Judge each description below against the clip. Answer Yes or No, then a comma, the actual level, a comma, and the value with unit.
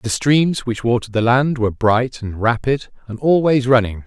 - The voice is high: No, low, 120 Hz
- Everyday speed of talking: Yes, average, 190 wpm